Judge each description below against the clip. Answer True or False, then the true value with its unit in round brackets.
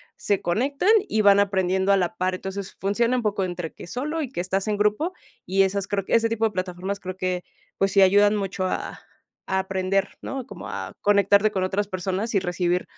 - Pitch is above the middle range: True (195 Hz)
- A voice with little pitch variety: True (2.0 semitones)